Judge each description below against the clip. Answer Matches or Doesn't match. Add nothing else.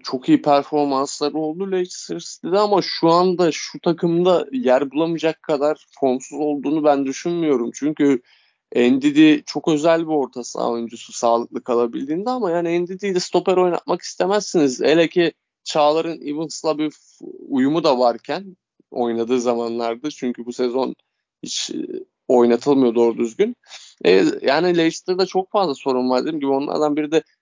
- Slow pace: Doesn't match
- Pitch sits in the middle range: Matches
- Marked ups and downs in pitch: Matches